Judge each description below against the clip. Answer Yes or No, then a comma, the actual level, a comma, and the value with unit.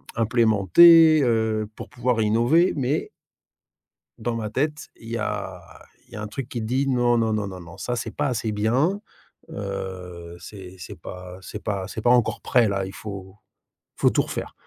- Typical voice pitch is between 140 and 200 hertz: No, low, 110 Hz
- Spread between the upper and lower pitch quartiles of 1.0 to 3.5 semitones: No, average, 4.0 semitones